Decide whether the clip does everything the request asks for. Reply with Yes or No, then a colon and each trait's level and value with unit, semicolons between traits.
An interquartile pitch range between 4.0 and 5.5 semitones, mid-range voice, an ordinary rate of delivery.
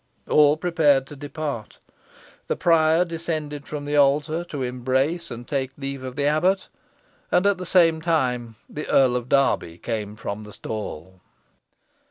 Yes: average, 4.4 semitones; medium, 145 Hz; average, 155 wpm